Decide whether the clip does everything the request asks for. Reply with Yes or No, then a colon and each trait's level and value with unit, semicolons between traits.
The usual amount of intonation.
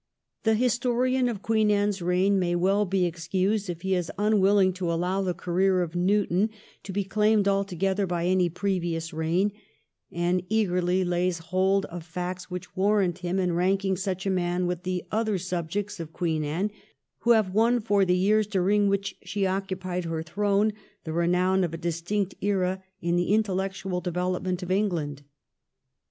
No: narrow, 2.3 semitones